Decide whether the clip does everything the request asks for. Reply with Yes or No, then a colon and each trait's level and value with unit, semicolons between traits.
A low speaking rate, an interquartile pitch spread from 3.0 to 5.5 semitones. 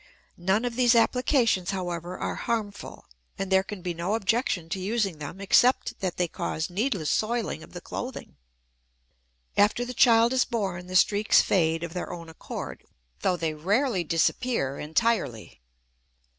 No: average, 155 wpm; average, 5.0 semitones